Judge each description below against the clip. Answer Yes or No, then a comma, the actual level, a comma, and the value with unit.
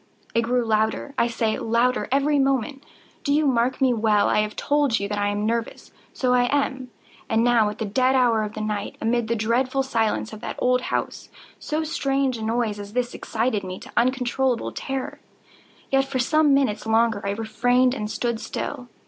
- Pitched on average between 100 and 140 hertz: No, high, 240 Hz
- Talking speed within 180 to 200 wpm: Yes, average, 190 wpm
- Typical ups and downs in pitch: Yes, average, 3.2 semitones